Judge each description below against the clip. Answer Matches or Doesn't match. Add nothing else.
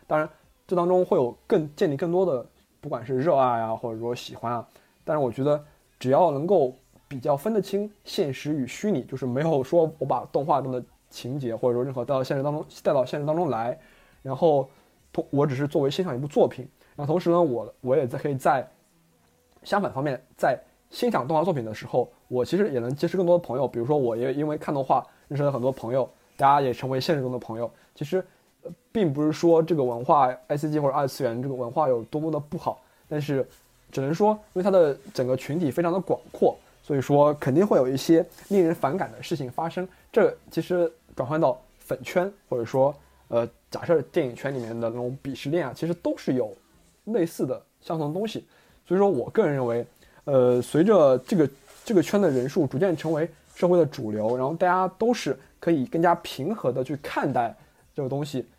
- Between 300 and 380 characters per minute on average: Matches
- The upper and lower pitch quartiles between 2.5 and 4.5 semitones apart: Doesn't match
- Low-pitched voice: Doesn't match